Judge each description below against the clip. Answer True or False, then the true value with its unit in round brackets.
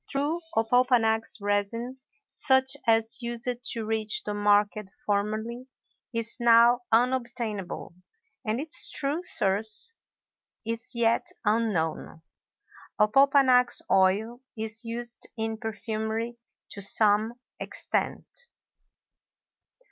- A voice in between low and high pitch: False (225 Hz)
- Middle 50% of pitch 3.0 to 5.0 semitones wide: False (2.4 semitones)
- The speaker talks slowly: True (90 wpm)